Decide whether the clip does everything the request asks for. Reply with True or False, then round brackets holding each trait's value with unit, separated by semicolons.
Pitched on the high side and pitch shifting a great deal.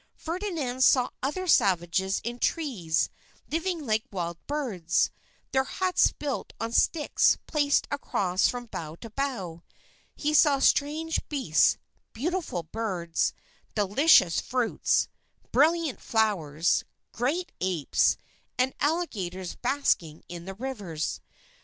True (245 Hz; 8.2 semitones)